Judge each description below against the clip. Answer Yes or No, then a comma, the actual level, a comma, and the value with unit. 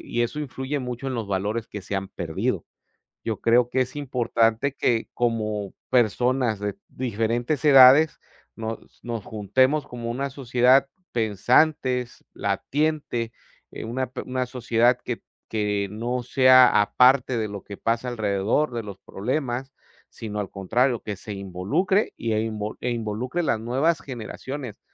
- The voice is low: Yes, low, 120 Hz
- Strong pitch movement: No, average, 3.2 semitones